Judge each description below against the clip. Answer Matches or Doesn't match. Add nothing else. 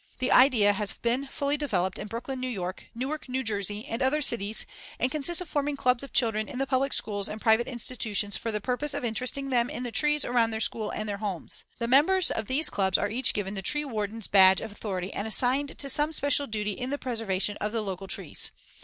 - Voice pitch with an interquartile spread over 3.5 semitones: Matches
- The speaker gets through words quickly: Matches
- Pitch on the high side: Matches